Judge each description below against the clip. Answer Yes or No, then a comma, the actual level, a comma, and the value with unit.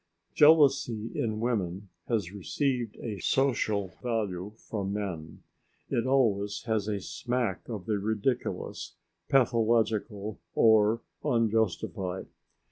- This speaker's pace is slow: Yes, slow, 100 wpm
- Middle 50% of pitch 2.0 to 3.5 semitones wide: Yes, average, 2.8 semitones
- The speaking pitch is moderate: No, low, 110 Hz